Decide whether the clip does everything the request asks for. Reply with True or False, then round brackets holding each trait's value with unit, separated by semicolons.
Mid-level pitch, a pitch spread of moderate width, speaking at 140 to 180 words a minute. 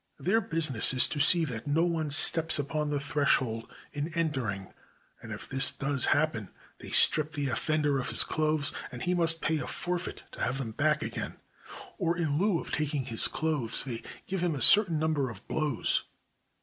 False (150 Hz; 3.3 semitones; 190 wpm)